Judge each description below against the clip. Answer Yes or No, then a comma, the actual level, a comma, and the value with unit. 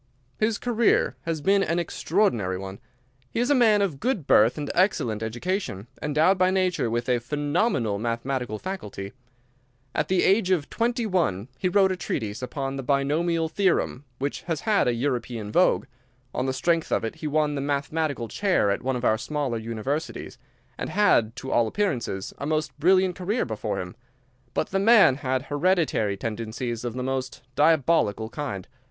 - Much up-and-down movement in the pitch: Yes, wide, 7.8 semitones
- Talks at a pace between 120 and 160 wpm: No, average, 170 wpm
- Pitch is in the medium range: Yes, medium, 145 Hz